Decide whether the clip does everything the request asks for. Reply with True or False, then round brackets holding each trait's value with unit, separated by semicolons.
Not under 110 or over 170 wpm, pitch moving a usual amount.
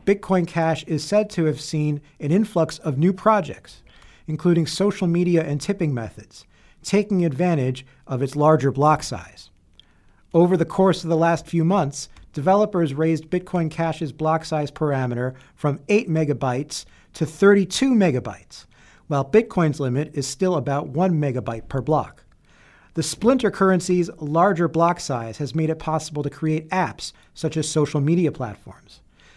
True (150 wpm; 4.0 semitones)